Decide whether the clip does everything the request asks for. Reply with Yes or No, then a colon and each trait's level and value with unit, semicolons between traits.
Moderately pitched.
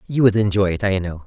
No: low, 100 Hz